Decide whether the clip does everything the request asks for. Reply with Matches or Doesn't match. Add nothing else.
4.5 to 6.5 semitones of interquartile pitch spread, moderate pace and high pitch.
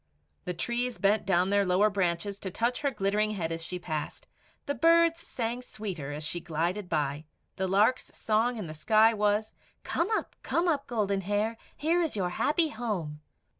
Matches